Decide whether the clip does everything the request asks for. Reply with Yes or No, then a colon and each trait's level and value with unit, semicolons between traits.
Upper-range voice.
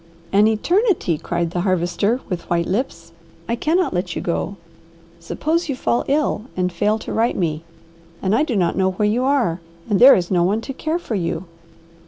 Yes: high, 205 Hz